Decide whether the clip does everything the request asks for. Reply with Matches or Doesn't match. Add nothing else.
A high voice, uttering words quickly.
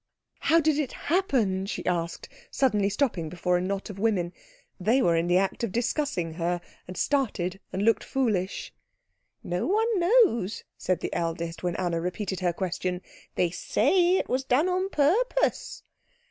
Doesn't match